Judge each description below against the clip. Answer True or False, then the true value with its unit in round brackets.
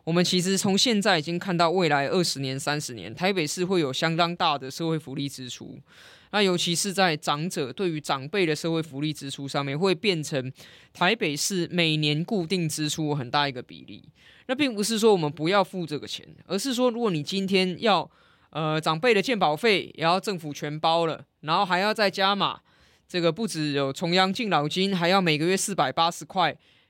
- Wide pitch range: False (4.3 semitones)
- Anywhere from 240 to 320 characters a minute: True (300 characters per minute)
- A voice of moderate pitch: True (170 Hz)